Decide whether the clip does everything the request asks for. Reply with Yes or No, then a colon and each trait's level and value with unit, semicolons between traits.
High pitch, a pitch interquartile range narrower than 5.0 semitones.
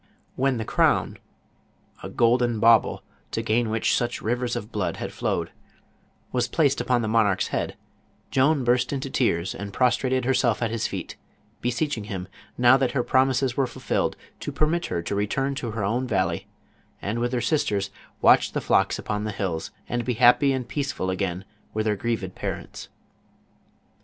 No: low, 120 Hz; average, 3.6 semitones